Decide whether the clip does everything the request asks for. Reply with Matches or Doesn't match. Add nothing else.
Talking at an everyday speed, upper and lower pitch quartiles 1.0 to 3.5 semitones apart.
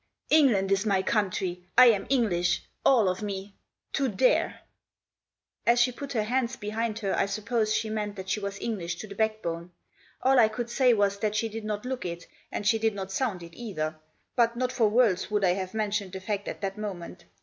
Doesn't match